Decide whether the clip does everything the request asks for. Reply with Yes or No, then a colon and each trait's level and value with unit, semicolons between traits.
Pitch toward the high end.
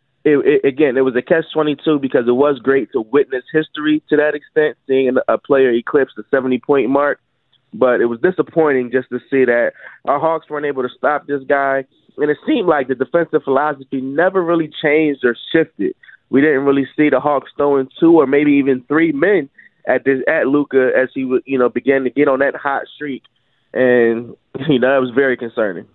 No: medium, 140 Hz